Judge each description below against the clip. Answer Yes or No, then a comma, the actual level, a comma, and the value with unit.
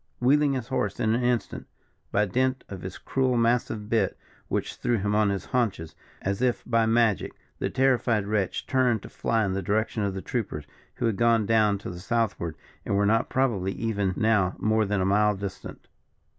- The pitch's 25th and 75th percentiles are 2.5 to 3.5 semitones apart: Yes, average, 3.2 semitones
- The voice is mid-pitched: No, low, 110 Hz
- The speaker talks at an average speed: Yes, average, 195 wpm